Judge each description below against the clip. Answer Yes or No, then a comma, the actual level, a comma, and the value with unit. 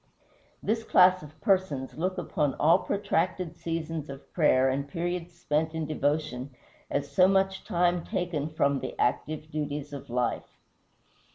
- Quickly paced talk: No, average, 145 wpm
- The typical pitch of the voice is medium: Yes, medium, 155 Hz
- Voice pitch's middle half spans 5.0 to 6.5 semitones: No, average, 3.8 semitones